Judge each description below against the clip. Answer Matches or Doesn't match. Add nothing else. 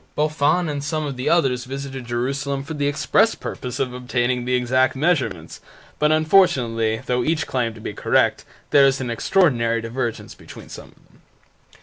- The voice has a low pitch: Matches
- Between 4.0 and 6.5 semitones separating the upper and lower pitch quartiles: Doesn't match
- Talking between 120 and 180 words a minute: Matches